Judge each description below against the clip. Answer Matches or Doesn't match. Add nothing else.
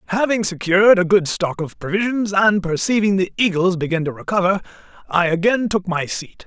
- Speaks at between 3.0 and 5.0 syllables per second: Doesn't match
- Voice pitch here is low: Doesn't match